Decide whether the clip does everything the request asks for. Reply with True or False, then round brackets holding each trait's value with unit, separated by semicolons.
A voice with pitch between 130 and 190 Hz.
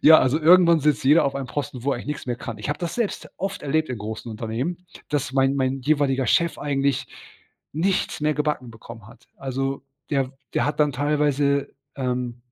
True (140 Hz)